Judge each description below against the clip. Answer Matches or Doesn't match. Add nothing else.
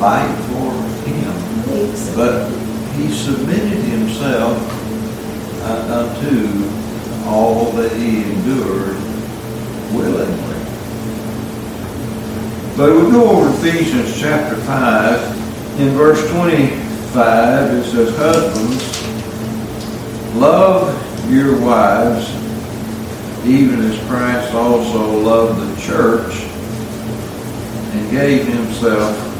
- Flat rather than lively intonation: Matches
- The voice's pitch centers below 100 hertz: Doesn't match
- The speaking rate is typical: Doesn't match